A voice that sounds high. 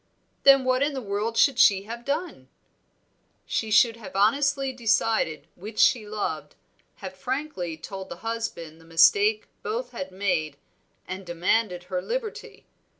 Yes: high, 220 Hz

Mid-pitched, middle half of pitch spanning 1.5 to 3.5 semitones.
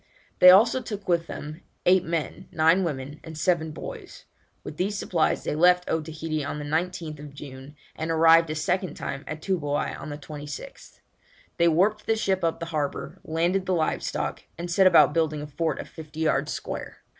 Yes: medium, 160 Hz; average, 2.9 semitones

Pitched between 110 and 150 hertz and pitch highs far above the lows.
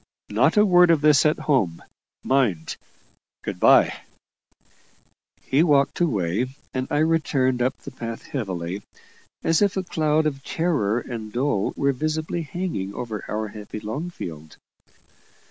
Yes: low, 135 Hz; wide, 6.7 semitones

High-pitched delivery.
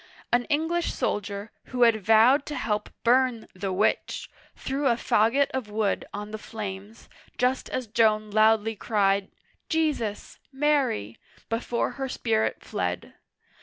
Yes: high, 225 Hz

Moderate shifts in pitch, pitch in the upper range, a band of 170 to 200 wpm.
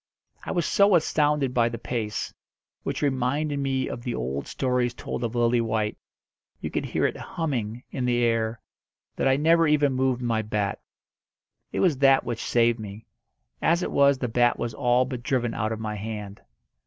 No: average, 3.4 semitones; low, 120 Hz; average, 180 wpm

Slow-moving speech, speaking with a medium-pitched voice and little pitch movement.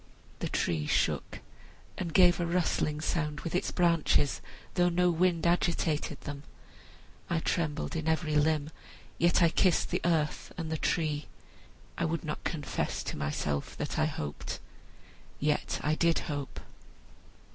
No: average, 145 wpm; medium, 160 Hz; narrow, 2.3 semitones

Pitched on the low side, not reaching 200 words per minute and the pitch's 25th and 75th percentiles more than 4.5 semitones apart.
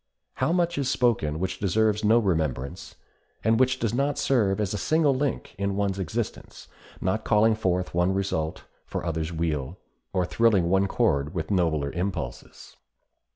Yes: very low, 95 Hz; average, 155 wpm; average, 5.1 semitones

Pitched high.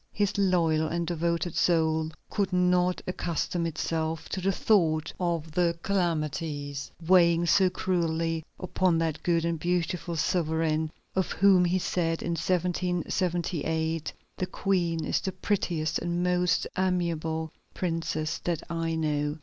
No: medium, 170 Hz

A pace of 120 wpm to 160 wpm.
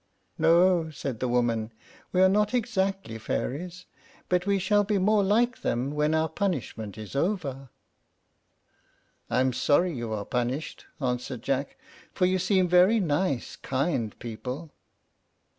Yes: average, 140 wpm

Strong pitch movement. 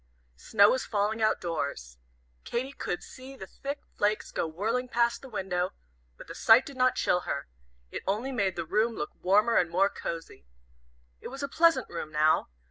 Yes: wide, 6.1 semitones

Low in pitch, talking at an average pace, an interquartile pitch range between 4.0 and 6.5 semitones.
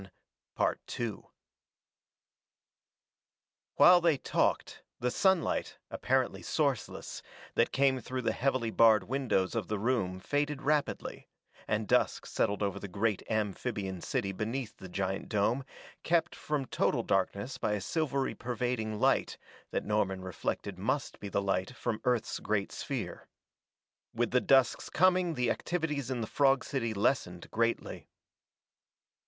No: low, 115 Hz; slow, 130 wpm; average, 5.0 semitones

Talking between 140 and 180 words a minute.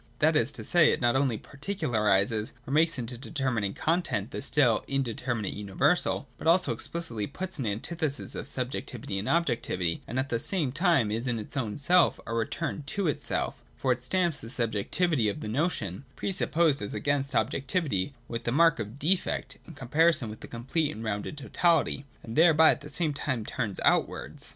No: average, 190 wpm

